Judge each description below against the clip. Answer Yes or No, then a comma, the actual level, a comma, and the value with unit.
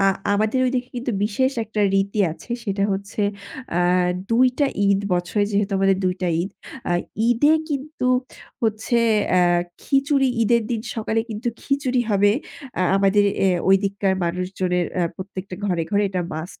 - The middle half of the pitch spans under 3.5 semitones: No, average, 4.2 semitones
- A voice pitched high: Yes, high, 205 Hz